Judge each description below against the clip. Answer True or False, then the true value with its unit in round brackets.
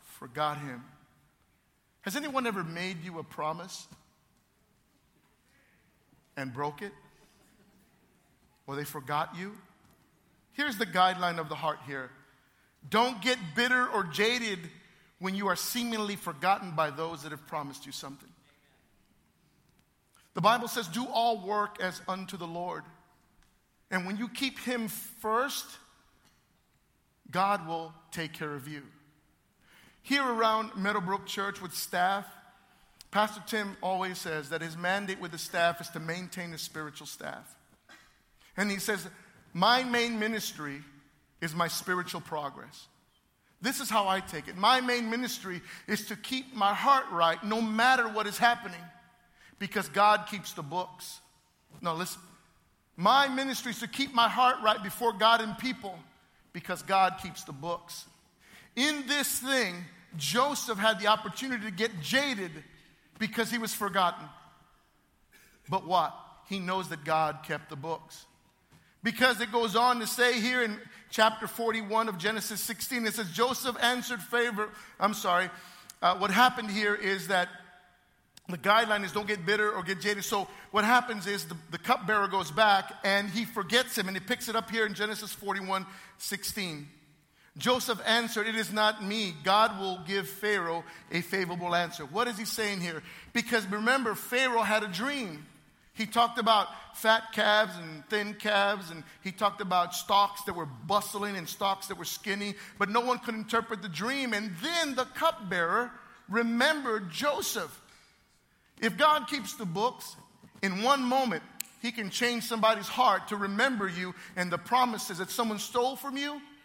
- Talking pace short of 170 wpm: True (155 wpm)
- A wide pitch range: False (4.6 semitones)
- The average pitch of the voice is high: True (205 Hz)